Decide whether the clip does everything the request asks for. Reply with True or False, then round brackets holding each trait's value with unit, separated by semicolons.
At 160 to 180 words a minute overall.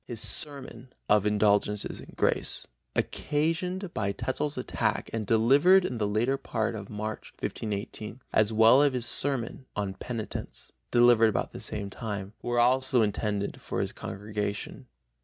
False (145 wpm)